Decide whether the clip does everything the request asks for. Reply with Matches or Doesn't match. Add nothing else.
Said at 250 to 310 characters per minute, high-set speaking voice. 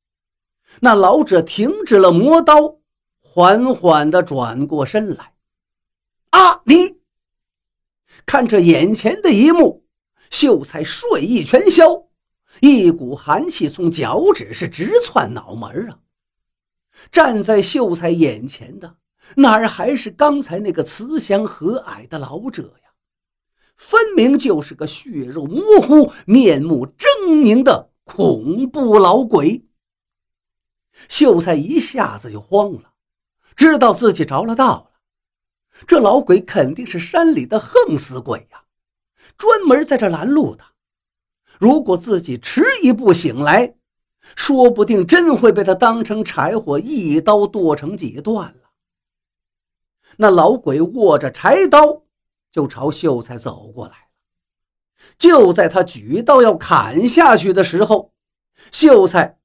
Doesn't match